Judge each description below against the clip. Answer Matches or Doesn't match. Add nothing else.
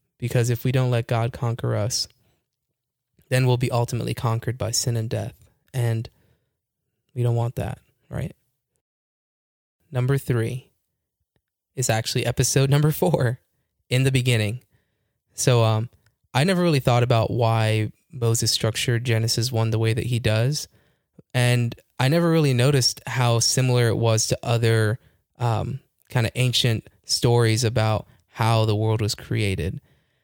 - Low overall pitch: Matches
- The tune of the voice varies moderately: Doesn't match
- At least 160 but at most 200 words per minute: Doesn't match